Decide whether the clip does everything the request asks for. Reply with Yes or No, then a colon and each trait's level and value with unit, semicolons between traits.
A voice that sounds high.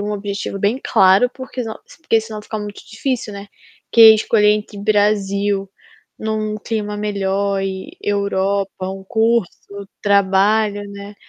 Yes: high, 205 Hz